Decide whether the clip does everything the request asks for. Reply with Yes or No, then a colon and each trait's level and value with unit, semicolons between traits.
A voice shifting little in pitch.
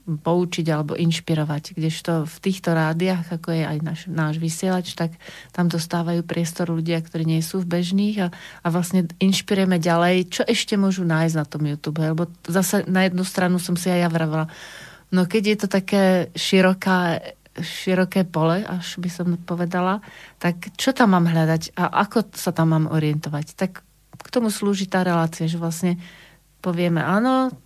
Yes: narrow, 2.3 semitones